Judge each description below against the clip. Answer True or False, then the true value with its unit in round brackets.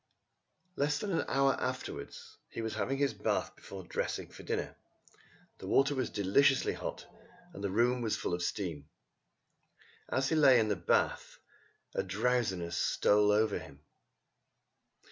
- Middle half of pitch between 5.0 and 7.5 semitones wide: True (5.5 semitones)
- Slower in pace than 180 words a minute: True (145 wpm)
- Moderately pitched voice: False (110 Hz)